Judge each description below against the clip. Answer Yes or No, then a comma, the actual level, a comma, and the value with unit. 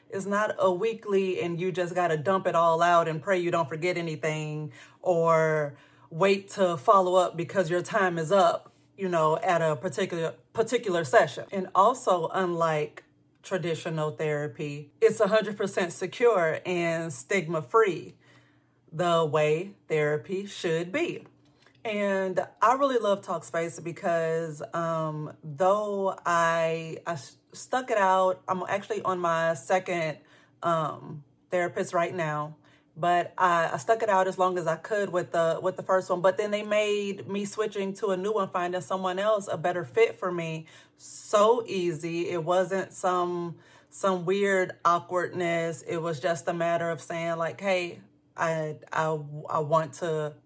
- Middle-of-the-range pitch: Yes, medium, 175 Hz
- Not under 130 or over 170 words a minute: Yes, average, 155 wpm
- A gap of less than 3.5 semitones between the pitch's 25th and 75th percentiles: Yes, average, 2.9 semitones